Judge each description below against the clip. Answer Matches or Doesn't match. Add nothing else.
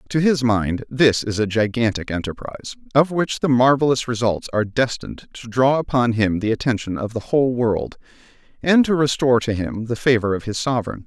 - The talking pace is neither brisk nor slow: Matches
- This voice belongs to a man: Matches